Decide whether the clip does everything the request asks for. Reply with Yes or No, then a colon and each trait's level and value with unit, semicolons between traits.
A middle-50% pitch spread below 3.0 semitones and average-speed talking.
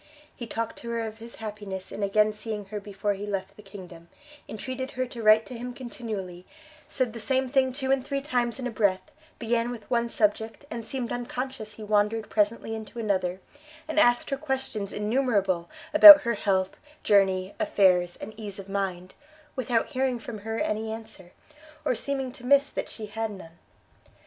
No: average, 3.5 semitones; average, 185 wpm